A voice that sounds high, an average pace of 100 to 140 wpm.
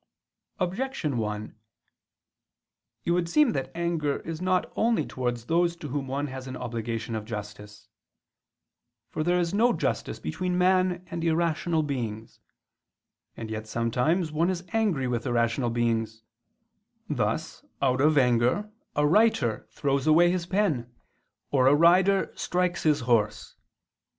No: medium, 145 Hz; slow, 135 wpm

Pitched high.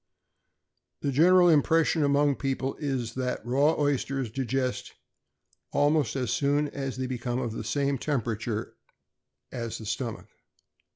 No: low, 135 Hz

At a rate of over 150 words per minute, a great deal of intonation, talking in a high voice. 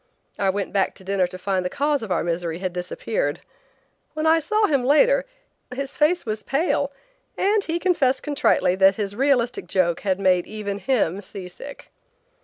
Yes: average, 175 wpm; wide, 7.6 semitones; high, 215 Hz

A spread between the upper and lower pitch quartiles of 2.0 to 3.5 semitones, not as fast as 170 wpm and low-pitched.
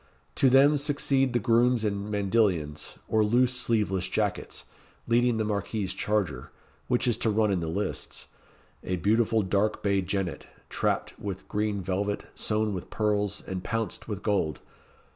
Yes: average, 2.9 semitones; average, 150 wpm; low, 105 Hz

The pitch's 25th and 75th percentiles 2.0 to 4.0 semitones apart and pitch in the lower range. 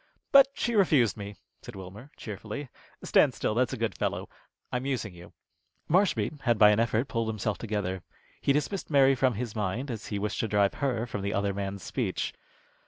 No: average, 4.7 semitones; low, 110 Hz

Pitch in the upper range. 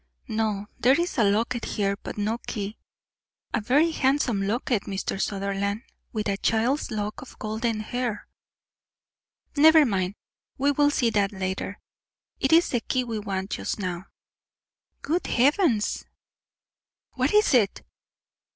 Yes: high, 220 Hz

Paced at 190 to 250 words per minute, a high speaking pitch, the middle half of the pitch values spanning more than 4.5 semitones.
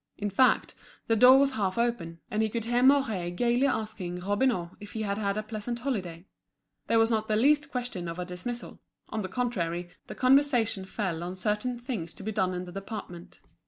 Yes: average, 195 wpm; high, 215 Hz; average, 4.9 semitones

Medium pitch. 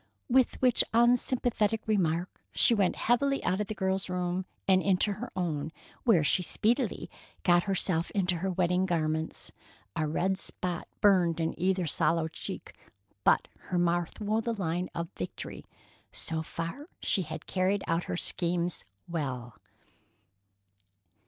Yes: medium, 180 Hz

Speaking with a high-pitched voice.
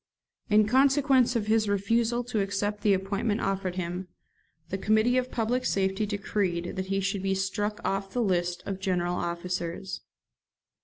Yes: high, 200 Hz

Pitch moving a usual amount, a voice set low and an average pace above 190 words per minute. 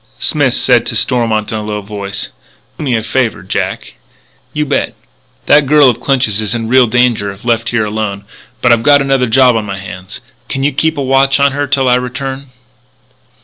Yes: average, 4.0 semitones; low, 125 Hz; average, 200 wpm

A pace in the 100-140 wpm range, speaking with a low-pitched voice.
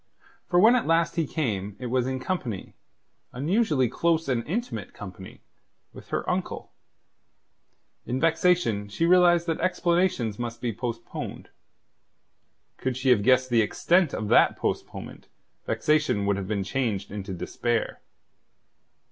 Yes: slow, 135 wpm; low, 130 Hz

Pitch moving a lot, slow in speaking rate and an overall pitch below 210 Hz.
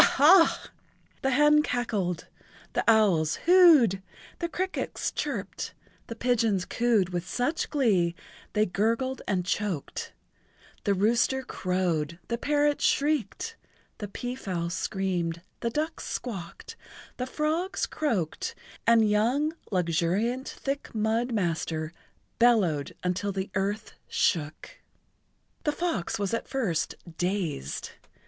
No: wide, 6.6 semitones; slow, 115 wpm; high, 215 Hz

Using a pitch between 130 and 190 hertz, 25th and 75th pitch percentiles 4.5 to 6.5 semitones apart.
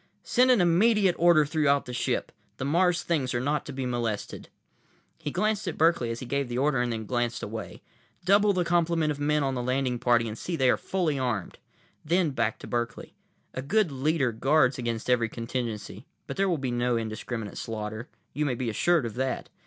Yes: low, 135 Hz; wide, 5.5 semitones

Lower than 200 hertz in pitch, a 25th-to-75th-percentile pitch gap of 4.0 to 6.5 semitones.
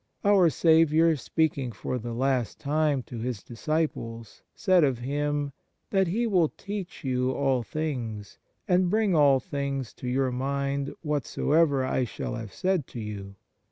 Yes: medium, 140 Hz; average, 4.3 semitones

